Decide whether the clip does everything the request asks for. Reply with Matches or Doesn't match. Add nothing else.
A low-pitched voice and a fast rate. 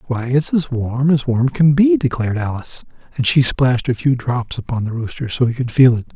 Matches